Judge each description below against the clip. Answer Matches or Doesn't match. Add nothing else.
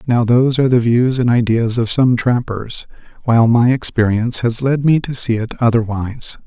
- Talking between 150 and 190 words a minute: Matches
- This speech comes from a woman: Doesn't match